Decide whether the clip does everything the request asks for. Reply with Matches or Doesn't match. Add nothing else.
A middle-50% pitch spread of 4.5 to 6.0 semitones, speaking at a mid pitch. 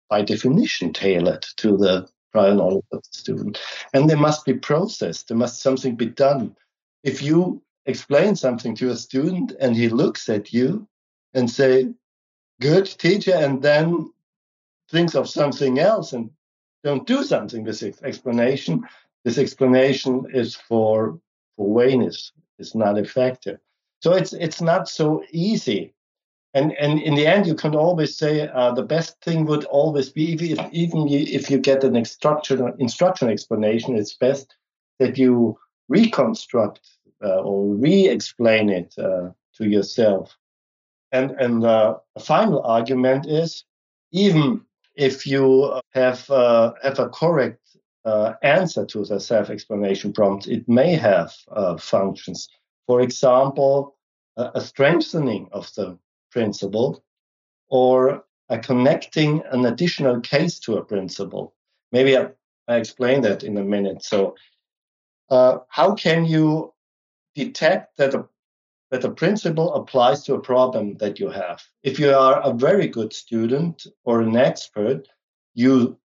Doesn't match